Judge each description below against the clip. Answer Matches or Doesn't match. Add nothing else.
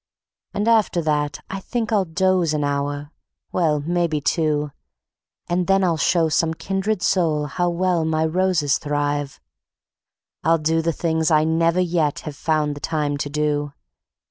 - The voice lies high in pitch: Doesn't match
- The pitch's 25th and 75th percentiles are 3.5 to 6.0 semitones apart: Doesn't match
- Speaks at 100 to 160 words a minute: Matches